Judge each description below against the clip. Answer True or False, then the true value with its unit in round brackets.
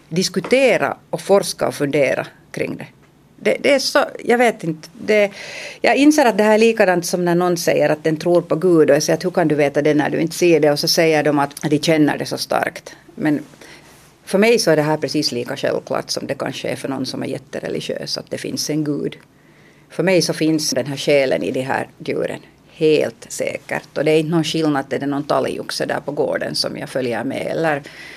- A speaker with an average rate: False (235 wpm)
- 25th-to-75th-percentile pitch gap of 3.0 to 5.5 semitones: True (4.1 semitones)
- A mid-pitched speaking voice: True (165 Hz)